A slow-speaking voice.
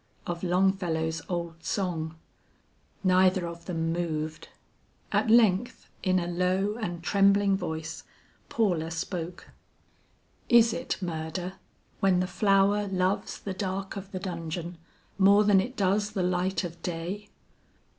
Yes: slow, 125 wpm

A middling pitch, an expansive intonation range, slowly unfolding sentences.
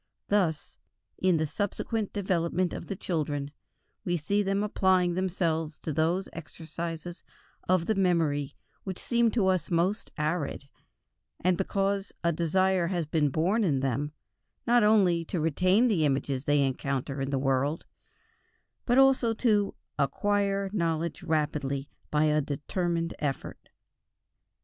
No: medium, 170 Hz; average, 4.4 semitones; slow, 130 wpm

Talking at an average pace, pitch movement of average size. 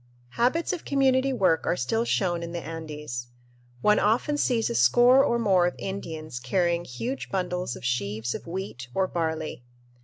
No: average, 165 wpm; wide, 7.2 semitones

